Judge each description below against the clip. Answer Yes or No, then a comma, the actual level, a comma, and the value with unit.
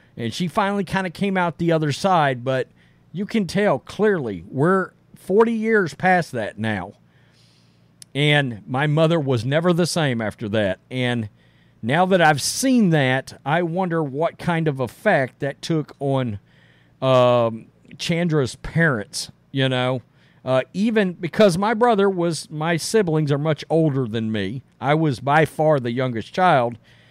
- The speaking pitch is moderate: Yes, medium, 155 Hz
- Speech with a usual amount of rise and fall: No, wide, 6.0 semitones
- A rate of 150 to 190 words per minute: Yes, average, 155 wpm